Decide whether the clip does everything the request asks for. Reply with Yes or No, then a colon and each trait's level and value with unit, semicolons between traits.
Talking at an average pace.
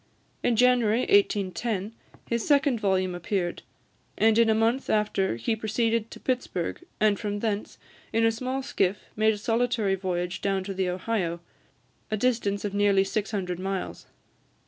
Yes: average, 150 wpm